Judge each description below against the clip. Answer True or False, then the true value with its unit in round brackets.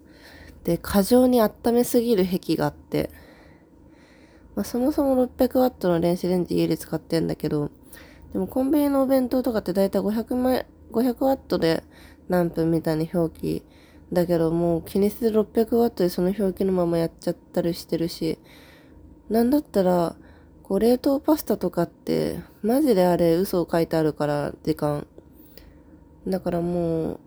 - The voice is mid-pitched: True (180 Hz)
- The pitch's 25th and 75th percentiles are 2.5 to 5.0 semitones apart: False (6.2 semitones)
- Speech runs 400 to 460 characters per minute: False (310 characters per minute)